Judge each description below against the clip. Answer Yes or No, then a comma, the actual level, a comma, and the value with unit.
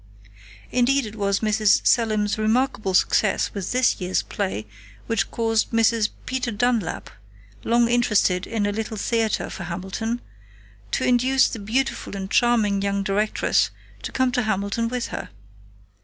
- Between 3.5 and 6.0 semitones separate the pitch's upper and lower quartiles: No, average, 3.1 semitones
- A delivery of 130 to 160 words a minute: Yes, average, 140 wpm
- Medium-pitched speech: No, high, 220 Hz